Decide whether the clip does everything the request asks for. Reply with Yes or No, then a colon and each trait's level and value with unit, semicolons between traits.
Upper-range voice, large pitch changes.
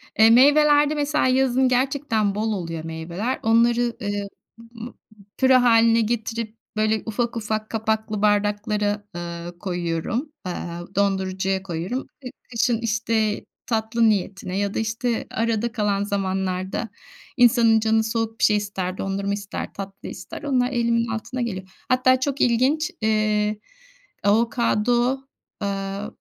No: high, 220 Hz; average, 3.0 semitones